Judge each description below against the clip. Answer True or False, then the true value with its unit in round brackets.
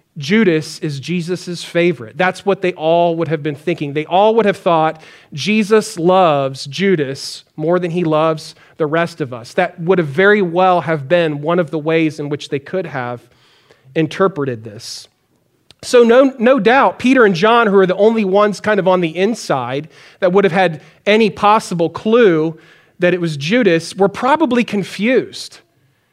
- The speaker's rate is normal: True (175 wpm)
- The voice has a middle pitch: True (175 Hz)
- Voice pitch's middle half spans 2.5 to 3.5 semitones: False (4.1 semitones)